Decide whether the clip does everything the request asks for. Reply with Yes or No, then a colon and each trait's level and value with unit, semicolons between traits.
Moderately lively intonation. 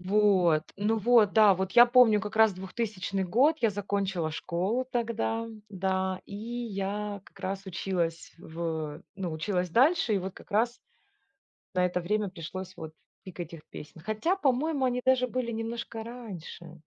Yes: average, 4.2 semitones